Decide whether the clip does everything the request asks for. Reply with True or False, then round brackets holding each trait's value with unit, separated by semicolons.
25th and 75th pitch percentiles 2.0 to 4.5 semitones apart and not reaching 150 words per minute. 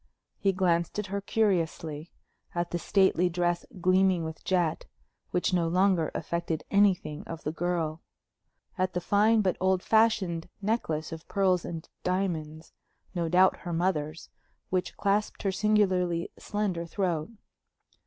True (2.7 semitones; 135 wpm)